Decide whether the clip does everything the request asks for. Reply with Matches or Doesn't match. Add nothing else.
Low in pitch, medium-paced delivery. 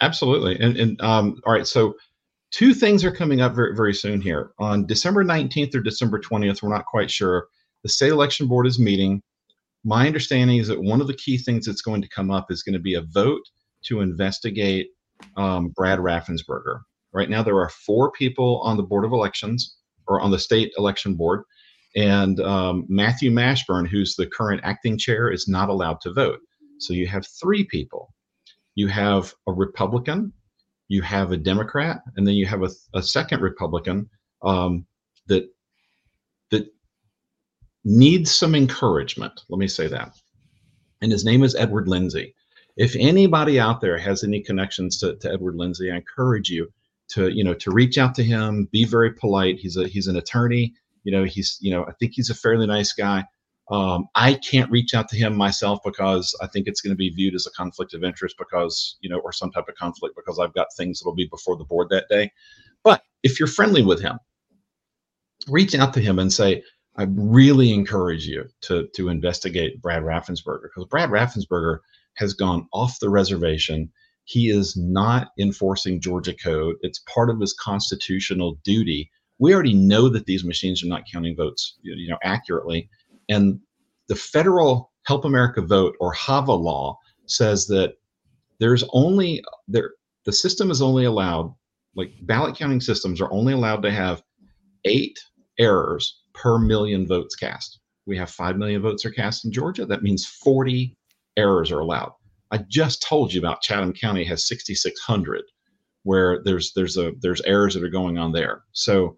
Matches